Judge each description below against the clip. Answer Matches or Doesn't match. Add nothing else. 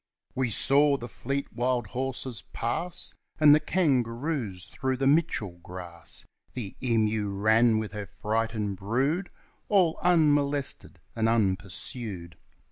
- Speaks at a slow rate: Matches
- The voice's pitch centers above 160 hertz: Doesn't match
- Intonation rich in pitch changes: Doesn't match